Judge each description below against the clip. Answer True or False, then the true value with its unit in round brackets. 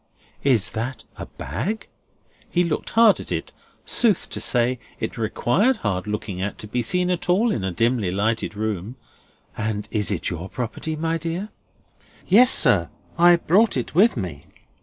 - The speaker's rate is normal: True (165 wpm)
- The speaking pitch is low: True (120 Hz)